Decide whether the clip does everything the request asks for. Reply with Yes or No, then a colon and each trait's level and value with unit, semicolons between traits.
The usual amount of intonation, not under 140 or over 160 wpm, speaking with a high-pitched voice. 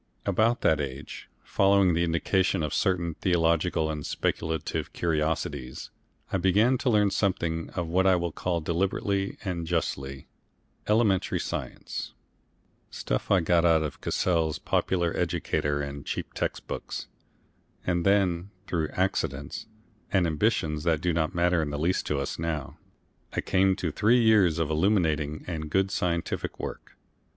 No: average, 3.3 semitones; average, 145 wpm; very low, 85 Hz